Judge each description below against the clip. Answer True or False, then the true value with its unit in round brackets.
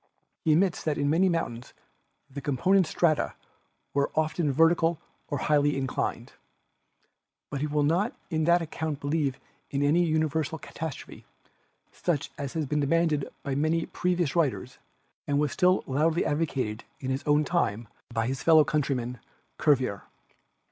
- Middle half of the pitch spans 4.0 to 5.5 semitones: False (2.9 semitones)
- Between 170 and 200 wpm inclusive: False (150 wpm)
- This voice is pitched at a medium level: True (150 Hz)